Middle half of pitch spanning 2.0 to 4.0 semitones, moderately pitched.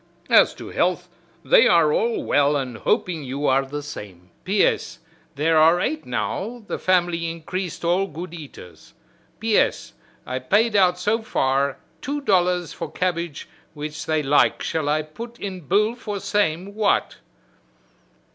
No: wide, 5.6 semitones; medium, 175 Hz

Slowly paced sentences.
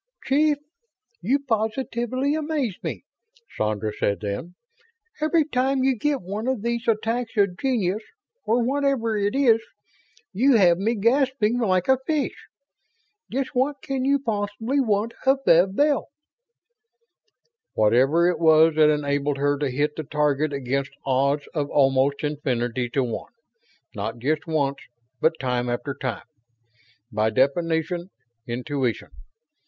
Yes: slow, 130 wpm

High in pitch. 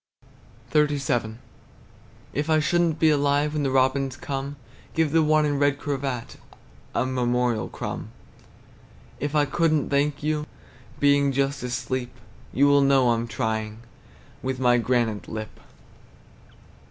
No: medium, 140 Hz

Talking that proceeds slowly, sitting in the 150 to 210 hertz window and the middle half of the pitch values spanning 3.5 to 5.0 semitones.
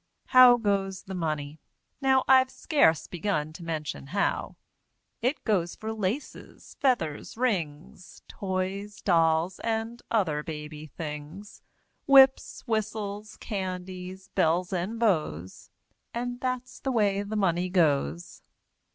No: slow, 115 wpm; high, 190 Hz; wide, 5.6 semitones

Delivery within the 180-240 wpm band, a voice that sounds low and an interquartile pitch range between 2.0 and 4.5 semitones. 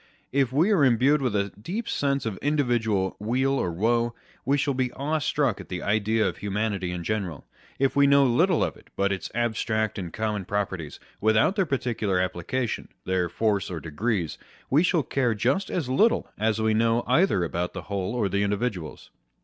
No: average, 190 wpm; low, 110 Hz; wide, 5.4 semitones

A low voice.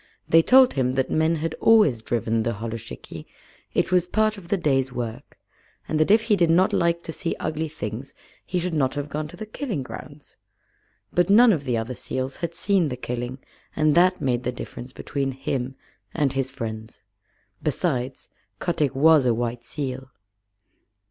No: medium, 145 Hz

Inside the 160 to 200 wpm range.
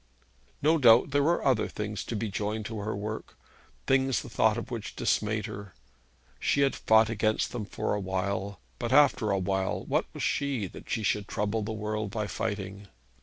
Yes: average, 185 wpm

